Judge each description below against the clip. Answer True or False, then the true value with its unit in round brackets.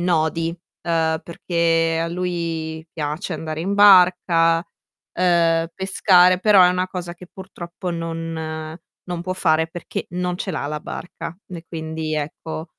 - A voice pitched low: False (170 Hz)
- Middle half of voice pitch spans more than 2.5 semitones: False (2.0 semitones)